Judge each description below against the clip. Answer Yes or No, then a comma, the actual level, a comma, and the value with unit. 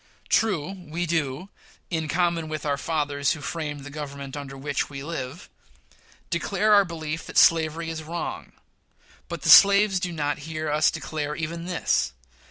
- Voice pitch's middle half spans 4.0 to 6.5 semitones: No, average, 2.7 semitones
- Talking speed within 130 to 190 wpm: Yes, average, 160 wpm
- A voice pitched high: No, medium, 160 Hz